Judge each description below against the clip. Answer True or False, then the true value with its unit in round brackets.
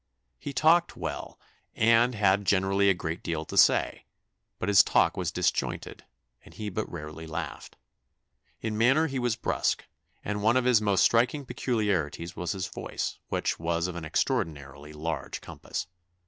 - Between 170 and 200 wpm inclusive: False (160 wpm)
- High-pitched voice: False (100 Hz)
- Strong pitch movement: True (5.7 semitones)